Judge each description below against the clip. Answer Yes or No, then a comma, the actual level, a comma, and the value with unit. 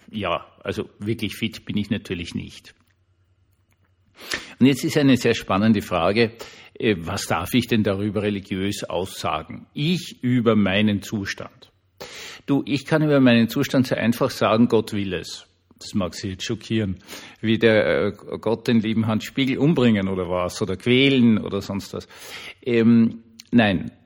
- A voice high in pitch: No, low, 110 Hz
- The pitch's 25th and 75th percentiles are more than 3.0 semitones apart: Yes, average, 3.4 semitones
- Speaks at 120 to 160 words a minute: Yes, average, 150 wpm